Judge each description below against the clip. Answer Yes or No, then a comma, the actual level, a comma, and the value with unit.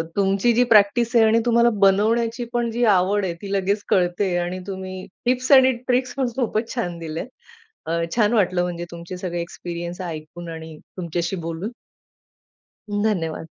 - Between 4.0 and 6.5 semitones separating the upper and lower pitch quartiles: Yes, average, 4.8 semitones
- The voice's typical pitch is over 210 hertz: No, high, 195 Hz